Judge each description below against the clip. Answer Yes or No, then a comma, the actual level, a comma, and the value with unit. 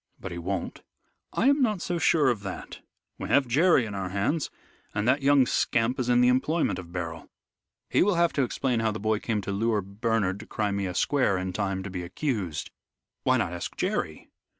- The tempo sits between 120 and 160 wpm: No, fast, 205 wpm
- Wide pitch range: Yes, wide, 5.8 semitones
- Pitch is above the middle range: No, low, 110 Hz